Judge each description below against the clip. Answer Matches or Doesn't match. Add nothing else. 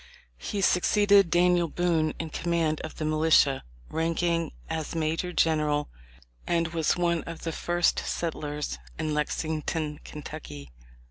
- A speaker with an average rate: Doesn't match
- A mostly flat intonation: Matches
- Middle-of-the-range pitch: Matches